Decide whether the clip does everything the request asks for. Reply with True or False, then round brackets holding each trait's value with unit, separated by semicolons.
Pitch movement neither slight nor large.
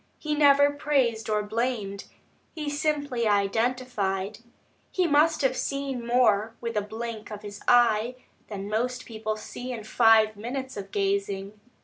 True (3.7 semitones)